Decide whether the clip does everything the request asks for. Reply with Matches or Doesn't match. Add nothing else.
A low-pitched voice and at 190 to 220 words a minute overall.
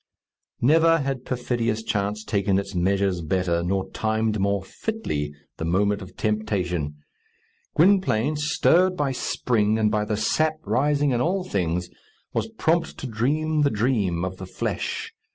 Doesn't match